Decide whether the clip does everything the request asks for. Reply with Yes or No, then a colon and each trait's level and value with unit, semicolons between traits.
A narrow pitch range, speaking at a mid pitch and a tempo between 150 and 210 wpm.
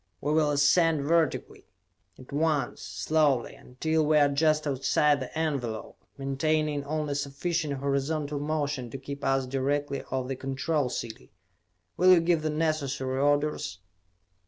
No: narrow, 2.3 semitones; medium, 145 Hz; slow, 135 wpm